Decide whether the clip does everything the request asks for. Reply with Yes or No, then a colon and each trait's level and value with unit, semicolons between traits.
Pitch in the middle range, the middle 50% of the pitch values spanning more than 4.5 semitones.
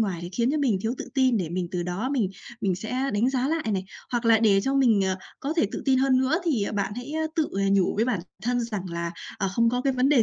No: high, 230 Hz; average, 5.1 semitones